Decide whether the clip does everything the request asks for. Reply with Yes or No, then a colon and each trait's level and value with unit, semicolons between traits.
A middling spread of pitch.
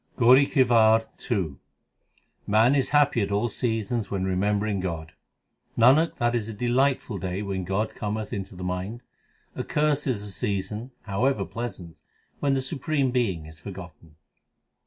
Yes: average, 4.7 semitones